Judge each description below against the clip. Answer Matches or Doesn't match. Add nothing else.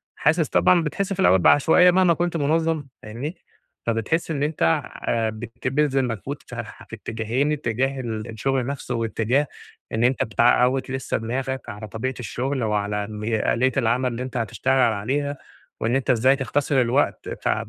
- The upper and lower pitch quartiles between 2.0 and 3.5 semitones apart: Doesn't match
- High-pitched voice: Doesn't match